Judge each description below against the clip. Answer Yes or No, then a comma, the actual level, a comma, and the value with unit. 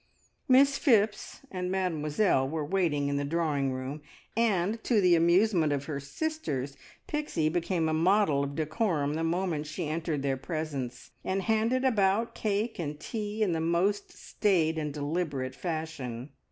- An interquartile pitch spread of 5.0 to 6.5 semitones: Yes, wide, 5.5 semitones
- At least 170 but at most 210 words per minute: No, average, 155 wpm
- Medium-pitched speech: Yes, medium, 165 Hz